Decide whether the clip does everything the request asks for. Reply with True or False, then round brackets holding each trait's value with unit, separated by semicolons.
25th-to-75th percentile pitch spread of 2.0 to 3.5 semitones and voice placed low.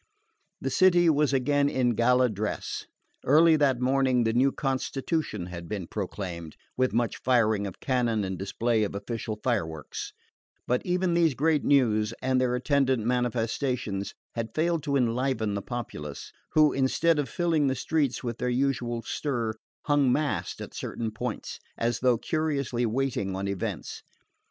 False (4.2 semitones; 125 Hz)